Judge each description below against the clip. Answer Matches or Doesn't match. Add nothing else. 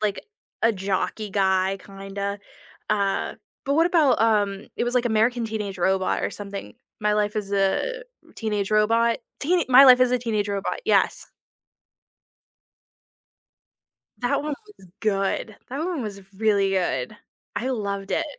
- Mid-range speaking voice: Doesn't match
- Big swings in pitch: Doesn't match